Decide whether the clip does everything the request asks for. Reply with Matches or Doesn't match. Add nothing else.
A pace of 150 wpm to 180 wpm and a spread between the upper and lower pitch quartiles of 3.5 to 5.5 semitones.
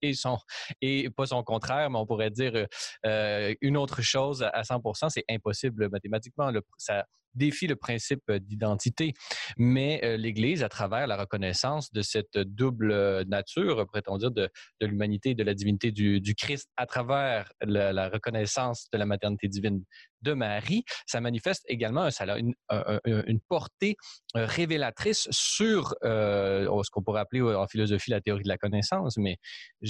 Matches